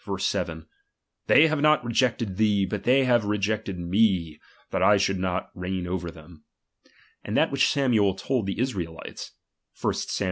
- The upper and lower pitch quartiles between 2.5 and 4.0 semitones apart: No, average, 4.8 semitones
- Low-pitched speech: Yes, low, 100 Hz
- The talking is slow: No, average, 165 wpm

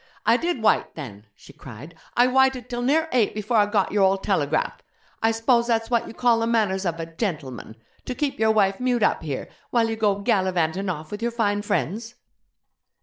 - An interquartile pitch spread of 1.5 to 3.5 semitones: No, average, 4.2 semitones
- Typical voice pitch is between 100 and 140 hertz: No, high, 215 Hz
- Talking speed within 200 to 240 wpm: Yes, fast, 205 wpm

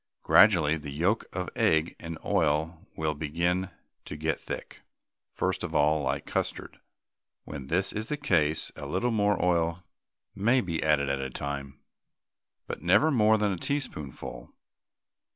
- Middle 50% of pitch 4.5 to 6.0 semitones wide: Yes, average, 5.0 semitones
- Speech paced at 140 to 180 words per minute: Yes, average, 150 wpm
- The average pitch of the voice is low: Yes, very low, 85 Hz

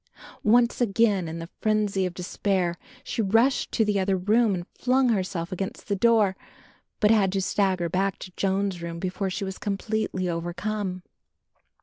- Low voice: No, high, 195 Hz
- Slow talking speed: No, average, 160 wpm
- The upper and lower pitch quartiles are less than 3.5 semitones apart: Yes, average, 2.7 semitones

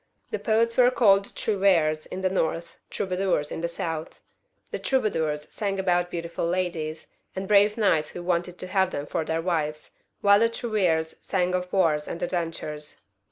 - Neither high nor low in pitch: Yes, medium, 180 Hz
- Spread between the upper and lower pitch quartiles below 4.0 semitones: Yes, average, 3.5 semitones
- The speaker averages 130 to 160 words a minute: No, average, 170 wpm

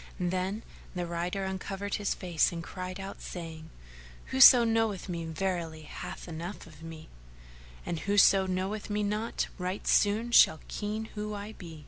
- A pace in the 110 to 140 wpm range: No, average, 150 wpm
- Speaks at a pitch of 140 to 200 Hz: Yes, high, 190 Hz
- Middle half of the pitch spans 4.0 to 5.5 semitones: No, average, 3.4 semitones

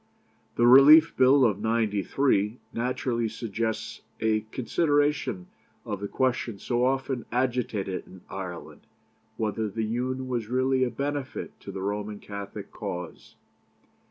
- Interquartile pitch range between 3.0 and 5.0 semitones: Yes, average, 3.9 semitones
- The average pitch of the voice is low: Yes, low, 115 Hz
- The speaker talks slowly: Yes, slow, 125 wpm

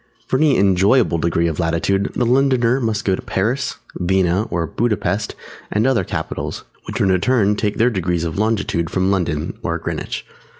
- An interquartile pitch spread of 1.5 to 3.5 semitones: No, average, 4.8 semitones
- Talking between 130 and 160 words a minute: No, average, 175 wpm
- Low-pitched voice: Yes, low, 100 Hz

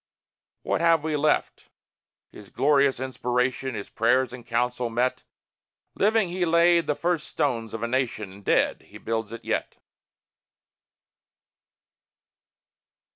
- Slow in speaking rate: Yes, slow, 125 wpm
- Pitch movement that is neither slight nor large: Yes, average, 4.9 semitones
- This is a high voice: No, low, 130 Hz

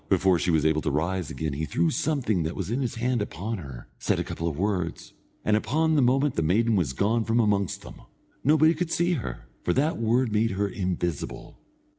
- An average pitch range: No, wide, 6.6 semitones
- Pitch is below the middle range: Yes, low, 105 Hz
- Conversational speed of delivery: No, fast, 215 wpm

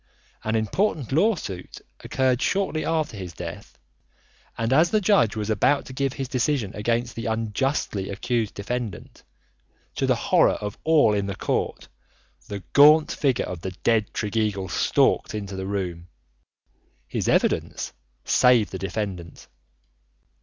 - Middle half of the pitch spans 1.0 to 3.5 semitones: No, average, 5.3 semitones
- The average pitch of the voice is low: Yes, low, 115 Hz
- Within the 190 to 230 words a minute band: No, slow, 135 wpm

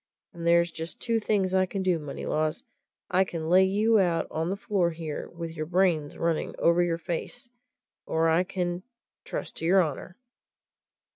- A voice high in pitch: No, medium, 175 Hz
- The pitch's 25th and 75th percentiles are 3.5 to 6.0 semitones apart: No, narrow, 2.6 semitones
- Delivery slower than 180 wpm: Yes, average, 170 wpm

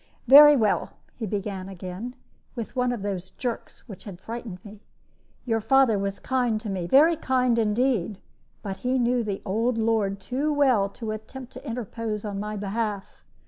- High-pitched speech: Yes, high, 220 Hz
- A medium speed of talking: Yes, average, 170 wpm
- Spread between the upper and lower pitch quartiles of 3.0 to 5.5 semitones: Yes, average, 3.8 semitones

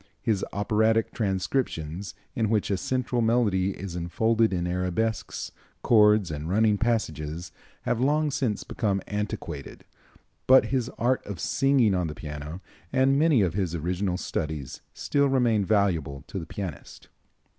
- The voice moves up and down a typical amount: Yes, average, 4.7 semitones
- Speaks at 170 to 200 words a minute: No, average, 140 wpm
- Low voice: Yes, low, 105 Hz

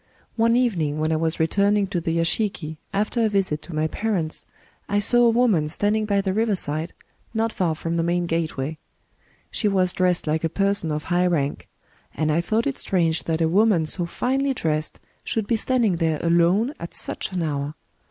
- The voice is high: No, medium, 175 Hz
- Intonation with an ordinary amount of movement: Yes, average, 4.7 semitones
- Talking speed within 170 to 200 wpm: Yes, average, 195 wpm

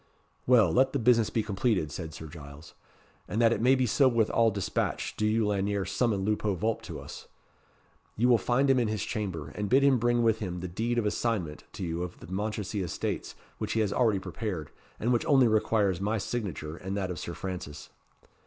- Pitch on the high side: No, low, 105 Hz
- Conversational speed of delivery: No, fast, 210 wpm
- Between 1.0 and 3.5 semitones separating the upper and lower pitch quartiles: No, average, 4.2 semitones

